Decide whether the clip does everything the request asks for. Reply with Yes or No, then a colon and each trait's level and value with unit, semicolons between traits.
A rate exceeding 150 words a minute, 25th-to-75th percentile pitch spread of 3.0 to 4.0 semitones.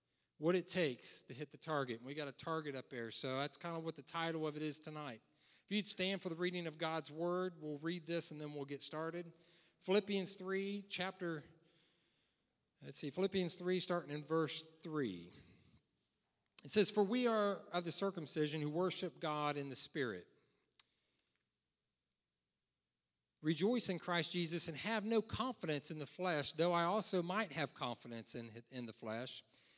Yes: average, 175 wpm; average, 3.7 semitones